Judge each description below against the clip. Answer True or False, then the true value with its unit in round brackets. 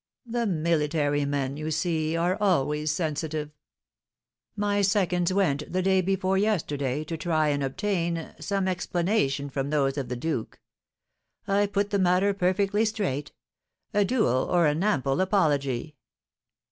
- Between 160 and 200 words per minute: False (135 wpm)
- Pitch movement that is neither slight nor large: True (4.9 semitones)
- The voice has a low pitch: False (170 Hz)